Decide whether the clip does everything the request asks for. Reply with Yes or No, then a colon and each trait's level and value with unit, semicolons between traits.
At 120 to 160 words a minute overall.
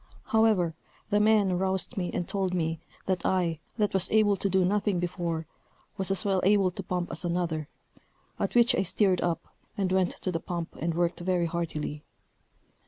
No: average, 180 wpm